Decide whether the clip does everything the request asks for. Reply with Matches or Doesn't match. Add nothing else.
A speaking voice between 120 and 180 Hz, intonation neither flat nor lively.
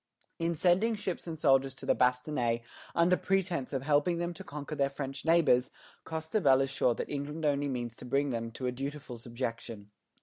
Matches